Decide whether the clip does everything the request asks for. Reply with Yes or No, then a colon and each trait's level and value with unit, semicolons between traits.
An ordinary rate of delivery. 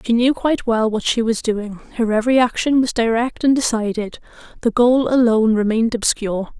Yes: average, 180 wpm